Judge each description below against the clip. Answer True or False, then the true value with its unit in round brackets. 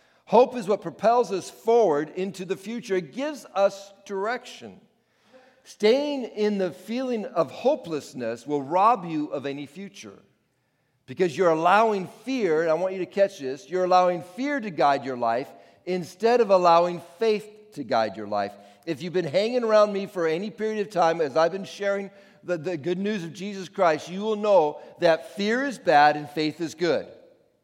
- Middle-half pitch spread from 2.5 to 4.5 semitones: False (5.2 semitones)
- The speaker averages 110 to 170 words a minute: False (180 wpm)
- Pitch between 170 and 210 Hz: True (185 Hz)